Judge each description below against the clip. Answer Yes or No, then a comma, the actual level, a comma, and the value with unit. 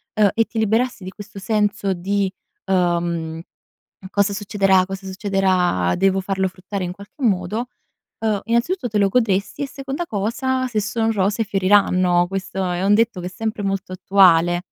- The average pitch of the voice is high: Yes, high, 195 Hz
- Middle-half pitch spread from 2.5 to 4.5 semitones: Yes, average, 2.8 semitones